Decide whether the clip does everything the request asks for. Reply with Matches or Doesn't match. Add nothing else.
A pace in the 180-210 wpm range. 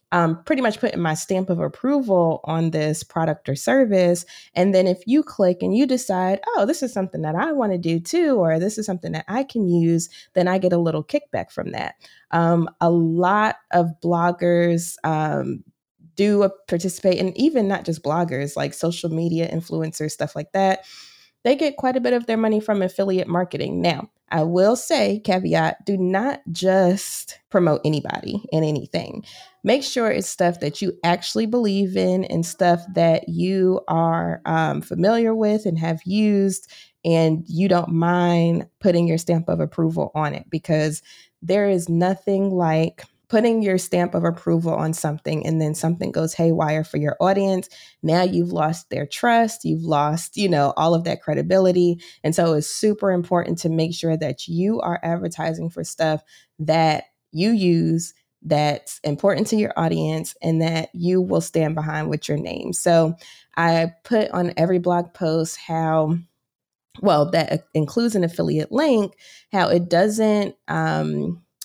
Doesn't match